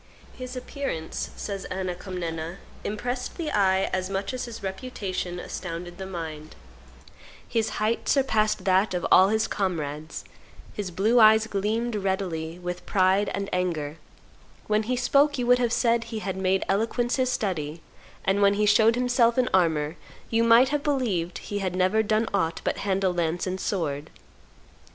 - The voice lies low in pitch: No, high, 195 Hz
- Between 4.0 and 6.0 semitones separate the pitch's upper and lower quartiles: Yes, average, 4.3 semitones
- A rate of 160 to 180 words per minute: Yes, average, 165 wpm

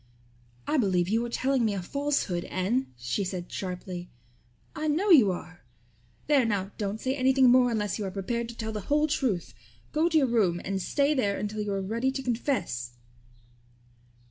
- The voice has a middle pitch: No, high, 220 Hz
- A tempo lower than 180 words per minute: No, average, 185 wpm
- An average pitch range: No, wide, 5.8 semitones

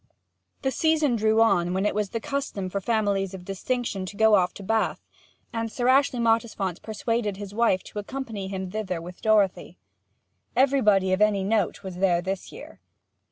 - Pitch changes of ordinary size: Yes, average, 3.2 semitones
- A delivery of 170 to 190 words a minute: Yes, average, 180 wpm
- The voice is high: Yes, high, 210 Hz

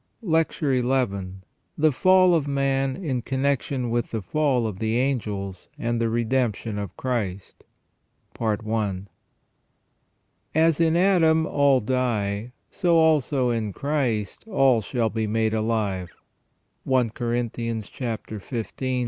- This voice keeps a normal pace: No, slow, 115 wpm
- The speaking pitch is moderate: No, low, 125 Hz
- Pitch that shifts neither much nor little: Yes, average, 4.3 semitones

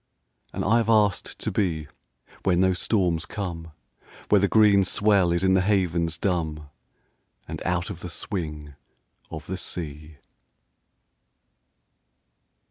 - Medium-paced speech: No, slow, 130 wpm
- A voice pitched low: Yes, very low, 90 Hz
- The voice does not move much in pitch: No, average, 3.3 semitones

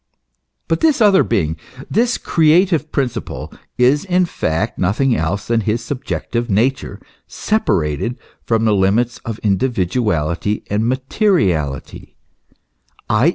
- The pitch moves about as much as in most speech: No, wide, 7.7 semitones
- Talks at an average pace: No, slow, 115 wpm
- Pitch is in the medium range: No, low, 115 Hz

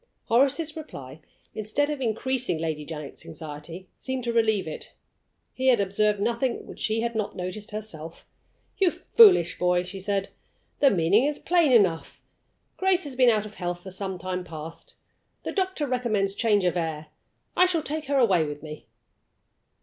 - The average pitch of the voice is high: Yes, high, 210 Hz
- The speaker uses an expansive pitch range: Yes, wide, 6.8 semitones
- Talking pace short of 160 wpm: No, average, 165 wpm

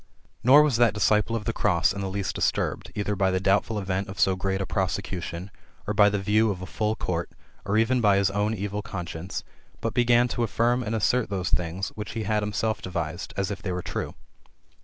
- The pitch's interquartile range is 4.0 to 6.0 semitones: No, narrow, 2.5 semitones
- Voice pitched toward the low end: Yes, low, 100 Hz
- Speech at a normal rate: No, fast, 220 wpm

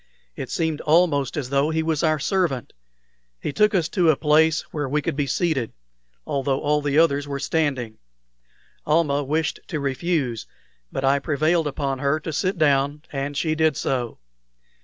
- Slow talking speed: No, average, 170 wpm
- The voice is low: No, medium, 150 Hz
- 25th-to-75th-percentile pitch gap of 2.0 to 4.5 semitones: Yes, narrow, 2.6 semitones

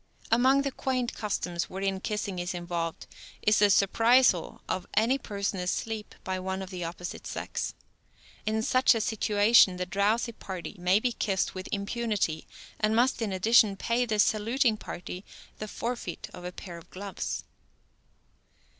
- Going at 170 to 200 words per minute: No, average, 155 wpm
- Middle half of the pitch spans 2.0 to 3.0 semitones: No, average, 3.8 semitones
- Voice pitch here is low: No, high, 205 Hz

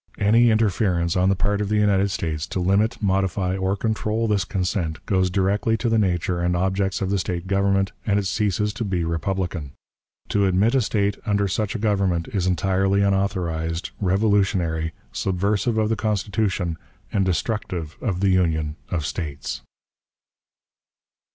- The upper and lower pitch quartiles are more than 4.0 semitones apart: No, narrow, 2.6 semitones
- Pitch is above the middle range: No, very low, 95 Hz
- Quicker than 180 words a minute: No, average, 155 wpm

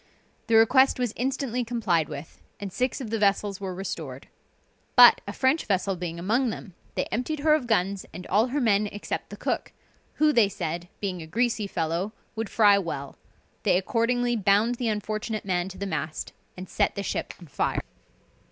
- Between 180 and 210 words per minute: Yes, average, 185 wpm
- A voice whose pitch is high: Yes, high, 205 Hz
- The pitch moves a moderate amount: Yes, average, 4.7 semitones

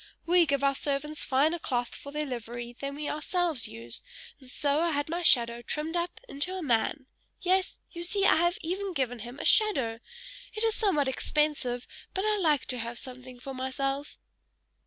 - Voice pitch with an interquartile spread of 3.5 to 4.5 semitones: No, average, 5.3 semitones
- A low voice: No, very high, 285 Hz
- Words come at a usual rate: Yes, average, 185 wpm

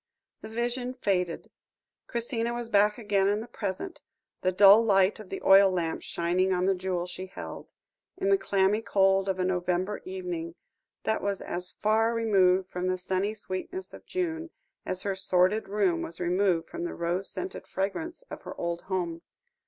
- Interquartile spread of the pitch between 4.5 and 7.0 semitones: No, average, 3.1 semitones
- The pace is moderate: Yes, average, 175 wpm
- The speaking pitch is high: Yes, high, 195 Hz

